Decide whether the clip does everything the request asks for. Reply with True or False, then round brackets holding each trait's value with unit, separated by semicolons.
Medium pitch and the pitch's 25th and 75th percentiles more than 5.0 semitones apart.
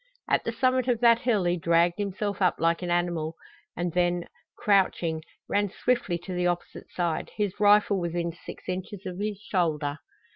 False (180 Hz; 3.1 semitones)